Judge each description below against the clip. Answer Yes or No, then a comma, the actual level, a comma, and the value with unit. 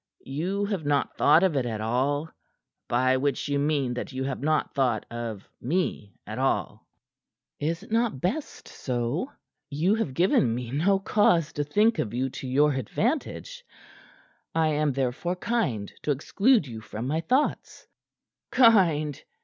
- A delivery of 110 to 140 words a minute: No, average, 150 wpm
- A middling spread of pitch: No, wide, 6.2 semitones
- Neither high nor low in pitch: Yes, medium, 145 Hz